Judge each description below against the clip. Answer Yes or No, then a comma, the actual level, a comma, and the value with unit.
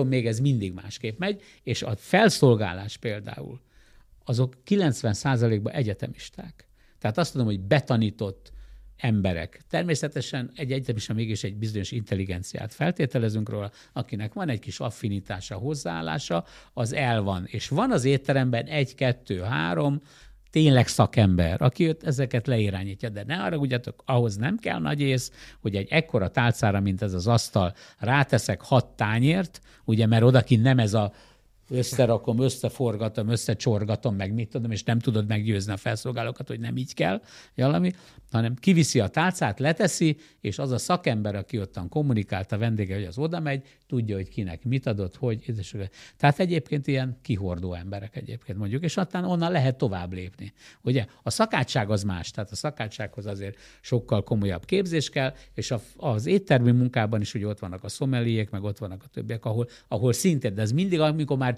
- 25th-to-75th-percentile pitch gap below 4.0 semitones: No, average, 4.5 semitones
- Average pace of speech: No, fast, 160 wpm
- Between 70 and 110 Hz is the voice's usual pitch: No, low, 120 Hz